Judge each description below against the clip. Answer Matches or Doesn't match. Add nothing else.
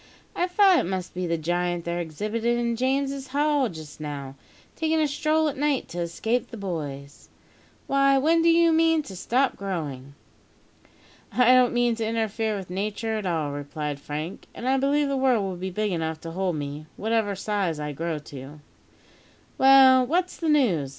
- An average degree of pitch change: Doesn't match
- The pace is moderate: Matches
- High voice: Matches